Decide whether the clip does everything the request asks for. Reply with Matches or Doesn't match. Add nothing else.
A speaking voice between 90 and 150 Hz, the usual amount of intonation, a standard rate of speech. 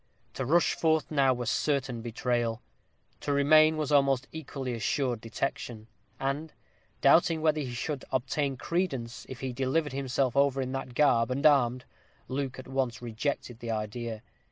Matches